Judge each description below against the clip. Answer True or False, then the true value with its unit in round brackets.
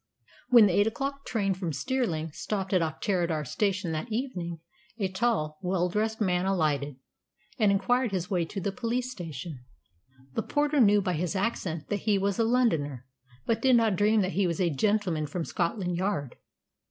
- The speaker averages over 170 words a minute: True (180 wpm)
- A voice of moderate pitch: False (195 Hz)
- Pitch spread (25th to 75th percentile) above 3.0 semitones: True (4.6 semitones)